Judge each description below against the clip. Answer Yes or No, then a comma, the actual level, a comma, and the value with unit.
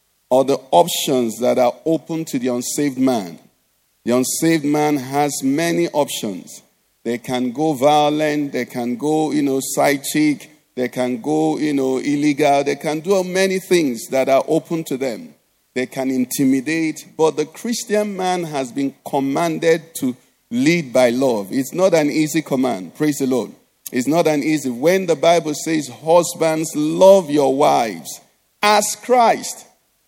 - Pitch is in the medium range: Yes, medium, 150 Hz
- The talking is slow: No, average, 155 wpm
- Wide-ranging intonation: No, average, 3.6 semitones